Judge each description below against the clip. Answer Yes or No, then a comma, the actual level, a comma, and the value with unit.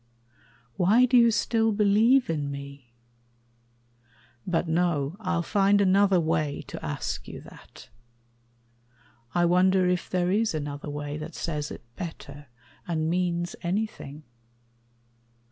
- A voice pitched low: No, medium, 175 Hz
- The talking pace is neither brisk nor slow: No, slow, 120 wpm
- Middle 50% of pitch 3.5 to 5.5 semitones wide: Yes, average, 4.7 semitones